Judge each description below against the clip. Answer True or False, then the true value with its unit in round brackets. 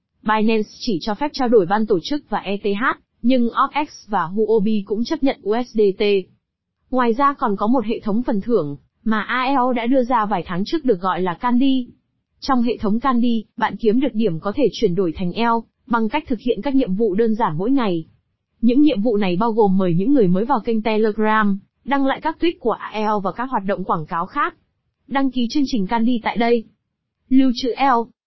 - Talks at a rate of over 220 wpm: False (215 wpm)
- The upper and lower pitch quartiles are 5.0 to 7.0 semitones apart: False (3.9 semitones)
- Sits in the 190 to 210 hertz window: False (225 Hz)